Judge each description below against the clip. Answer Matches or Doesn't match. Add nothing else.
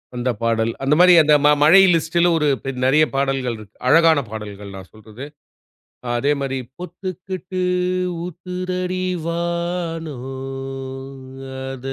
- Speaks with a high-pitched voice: Doesn't match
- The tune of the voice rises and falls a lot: Matches